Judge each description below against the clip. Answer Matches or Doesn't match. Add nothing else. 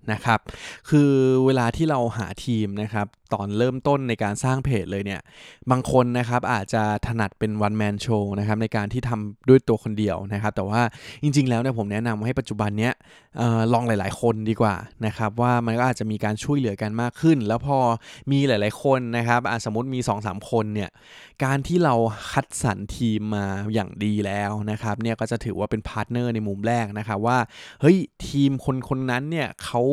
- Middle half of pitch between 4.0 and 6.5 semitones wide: Doesn't match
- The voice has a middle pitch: Doesn't match